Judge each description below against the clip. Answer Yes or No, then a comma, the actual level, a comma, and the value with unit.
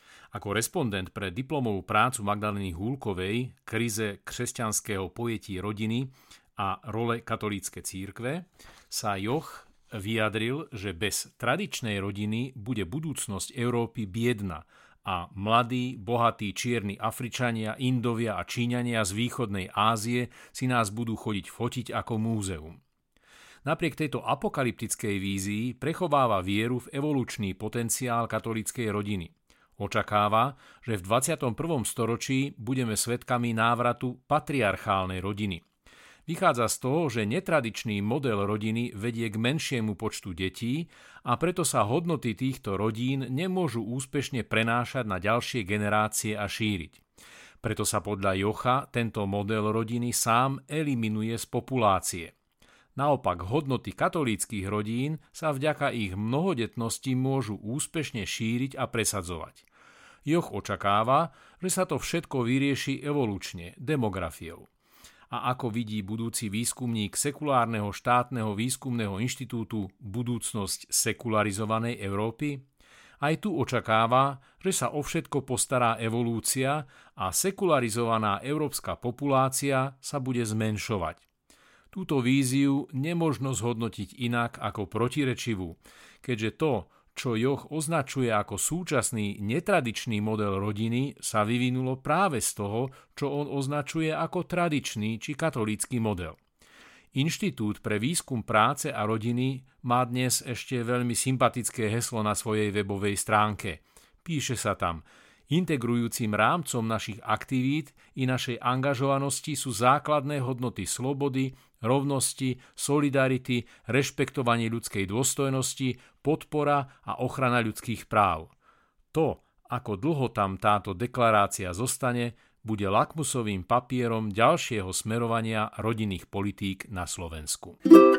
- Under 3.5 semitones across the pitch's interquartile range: No, average, 3.9 semitones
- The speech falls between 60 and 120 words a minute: Yes, slow, 110 wpm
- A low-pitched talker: Yes, low, 120 Hz